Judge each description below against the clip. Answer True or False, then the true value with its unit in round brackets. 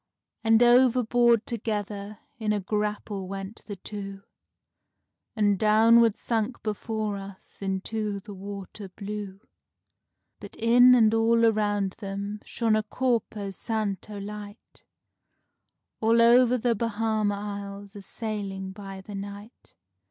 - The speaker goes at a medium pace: False (115 wpm)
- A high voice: True (210 Hz)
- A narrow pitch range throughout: True (2.1 semitones)